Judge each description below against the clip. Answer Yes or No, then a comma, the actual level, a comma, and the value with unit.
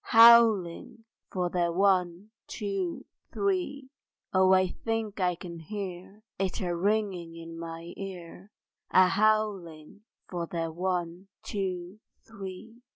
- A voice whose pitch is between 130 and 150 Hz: No, medium, 185 Hz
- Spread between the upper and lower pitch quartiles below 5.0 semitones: Yes, average, 3.4 semitones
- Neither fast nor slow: No, slow, 115 wpm